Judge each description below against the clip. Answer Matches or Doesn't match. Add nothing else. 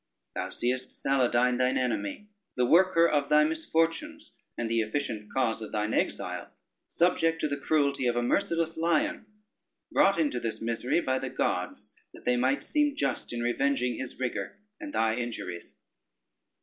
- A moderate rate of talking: Matches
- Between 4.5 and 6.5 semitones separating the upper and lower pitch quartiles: Matches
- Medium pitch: Doesn't match